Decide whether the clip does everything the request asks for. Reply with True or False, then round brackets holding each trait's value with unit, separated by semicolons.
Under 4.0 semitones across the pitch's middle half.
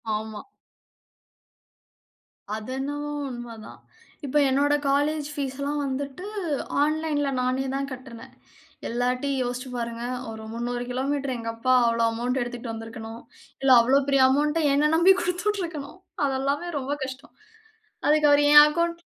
True (3.2 semitones)